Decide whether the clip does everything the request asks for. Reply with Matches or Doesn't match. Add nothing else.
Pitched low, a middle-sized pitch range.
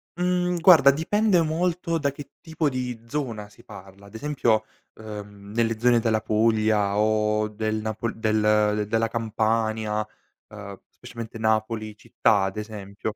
Matches